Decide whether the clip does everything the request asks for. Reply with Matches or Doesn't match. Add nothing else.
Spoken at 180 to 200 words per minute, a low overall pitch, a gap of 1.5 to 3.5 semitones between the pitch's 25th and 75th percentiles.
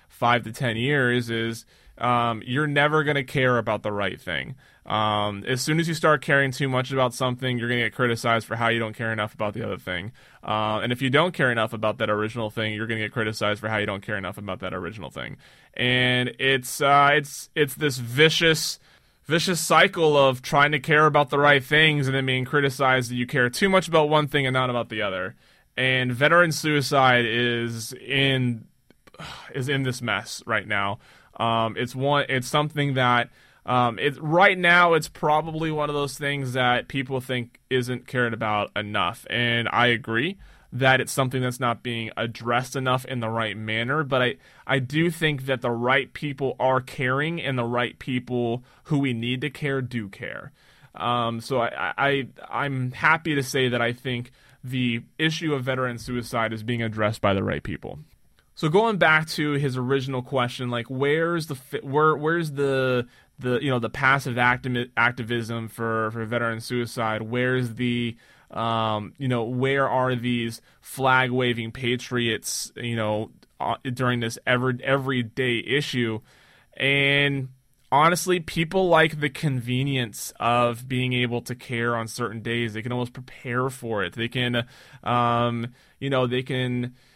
Matches